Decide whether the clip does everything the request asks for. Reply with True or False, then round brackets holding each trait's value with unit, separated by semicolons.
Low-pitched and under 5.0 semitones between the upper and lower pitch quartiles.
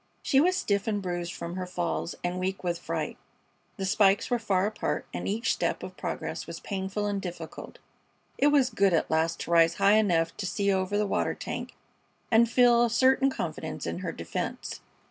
False (200 Hz; 3.9 semitones)